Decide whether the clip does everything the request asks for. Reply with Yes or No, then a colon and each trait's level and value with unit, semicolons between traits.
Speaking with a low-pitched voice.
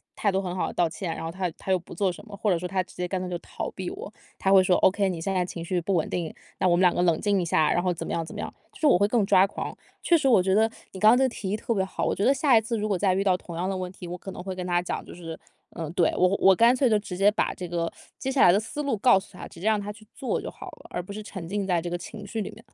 No: high, 190 Hz